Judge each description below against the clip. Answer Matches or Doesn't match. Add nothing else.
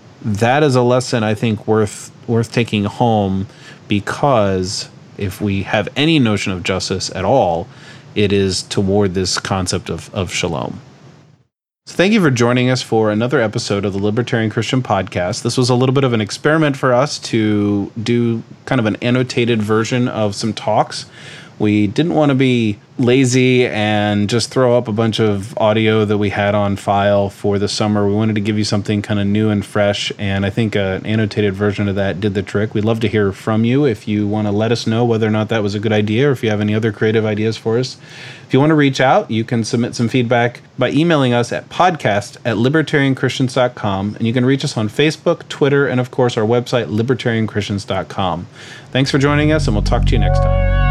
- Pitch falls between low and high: Doesn't match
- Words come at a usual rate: Doesn't match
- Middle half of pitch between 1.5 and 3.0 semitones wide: Doesn't match